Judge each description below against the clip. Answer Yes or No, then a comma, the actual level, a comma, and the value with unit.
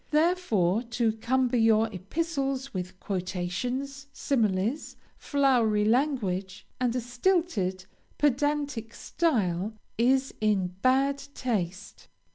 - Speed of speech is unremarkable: No, slow, 90 wpm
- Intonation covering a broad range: Yes, wide, 5.7 semitones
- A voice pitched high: Yes, high, 240 Hz